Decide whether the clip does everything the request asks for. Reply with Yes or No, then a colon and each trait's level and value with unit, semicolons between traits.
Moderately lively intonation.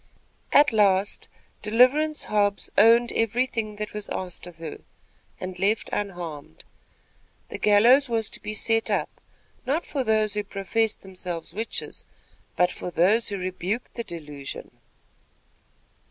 Yes: average, 3.7 semitones